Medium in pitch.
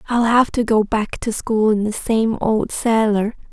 No: high, 220 Hz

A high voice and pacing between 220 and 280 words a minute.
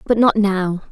No: high, 205 Hz; average, 200 wpm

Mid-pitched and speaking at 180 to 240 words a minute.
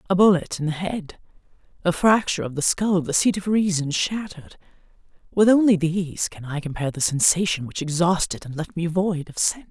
Yes: medium, 175 Hz; average, 185 wpm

